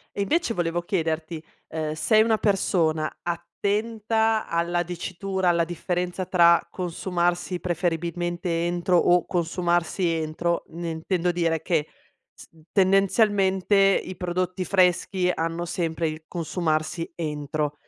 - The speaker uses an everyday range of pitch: No, narrow, 2.1 semitones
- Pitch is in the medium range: Yes, medium, 175 Hz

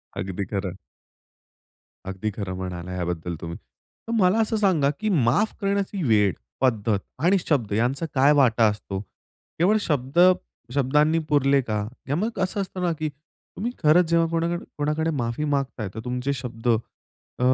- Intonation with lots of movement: Yes, wide, 7.5 semitones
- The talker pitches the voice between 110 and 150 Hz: Yes, medium, 140 Hz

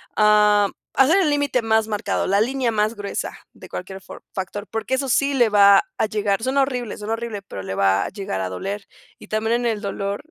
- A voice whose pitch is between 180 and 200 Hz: No, high, 210 Hz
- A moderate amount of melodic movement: Yes, average, 3.3 semitones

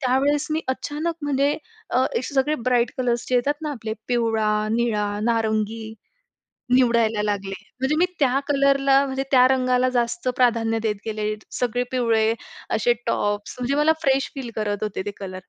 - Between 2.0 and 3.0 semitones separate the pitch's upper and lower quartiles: No, average, 3.6 semitones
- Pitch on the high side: Yes, high, 245 Hz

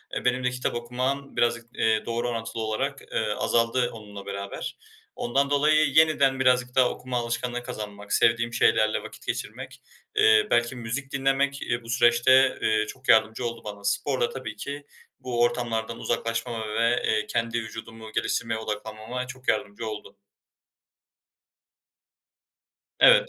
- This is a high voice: No, low, 120 Hz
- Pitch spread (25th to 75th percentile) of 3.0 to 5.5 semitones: No, narrow, 2.6 semitones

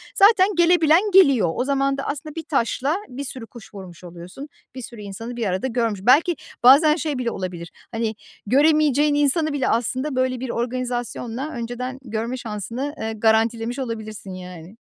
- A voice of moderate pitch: No, very high, 250 Hz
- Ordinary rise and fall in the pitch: Yes, average, 4.3 semitones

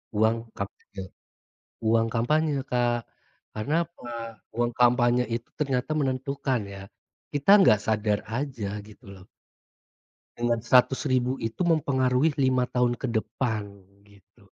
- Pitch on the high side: No, low, 120 Hz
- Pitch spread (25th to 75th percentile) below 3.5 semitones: Yes, average, 3.0 semitones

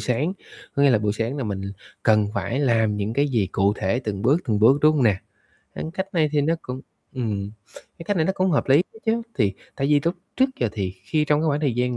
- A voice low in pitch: Yes, low, 130 Hz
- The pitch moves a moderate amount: No, wide, 6.2 semitones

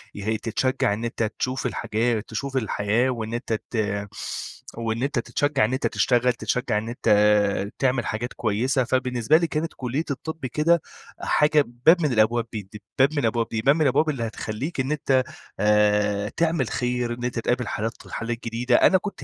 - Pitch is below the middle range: Yes, low, 120 Hz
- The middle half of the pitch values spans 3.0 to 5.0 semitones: Yes, average, 3.5 semitones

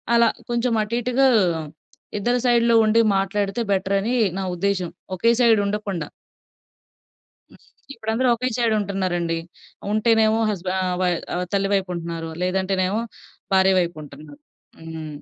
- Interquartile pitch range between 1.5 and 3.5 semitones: No, average, 4.1 semitones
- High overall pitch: Yes, high, 195 Hz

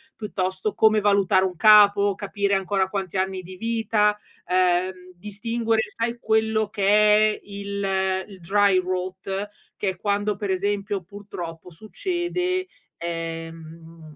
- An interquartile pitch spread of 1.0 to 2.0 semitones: No, narrow, 2.4 semitones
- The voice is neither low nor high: No, high, 200 Hz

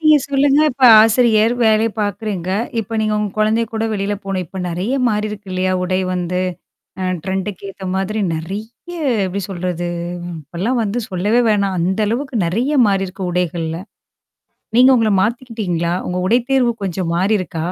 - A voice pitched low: No, high, 200 Hz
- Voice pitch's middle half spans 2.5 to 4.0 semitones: Yes, average, 3.5 semitones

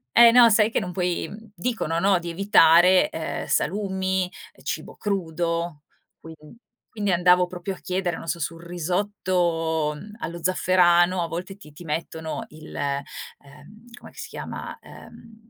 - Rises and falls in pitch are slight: No, average, 3.1 semitones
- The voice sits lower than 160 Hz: No, medium, 180 Hz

